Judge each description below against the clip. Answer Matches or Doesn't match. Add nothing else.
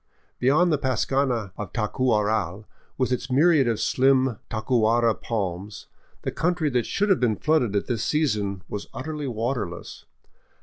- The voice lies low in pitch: Matches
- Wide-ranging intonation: Doesn't match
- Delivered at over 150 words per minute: Doesn't match